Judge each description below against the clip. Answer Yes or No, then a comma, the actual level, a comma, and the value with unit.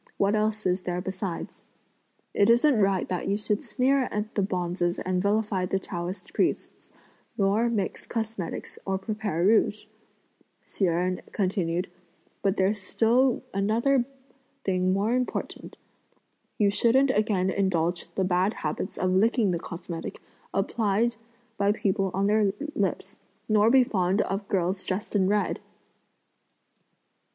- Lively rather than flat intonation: No, average, 2.7 semitones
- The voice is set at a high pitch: Yes, high, 200 Hz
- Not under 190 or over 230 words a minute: No, slow, 135 wpm